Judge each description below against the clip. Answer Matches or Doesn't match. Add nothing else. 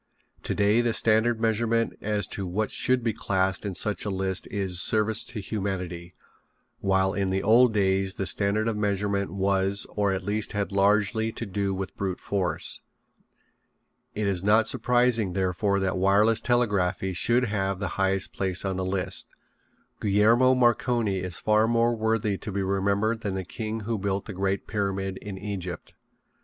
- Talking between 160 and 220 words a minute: Matches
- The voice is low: Matches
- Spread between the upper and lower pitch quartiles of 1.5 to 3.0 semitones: Matches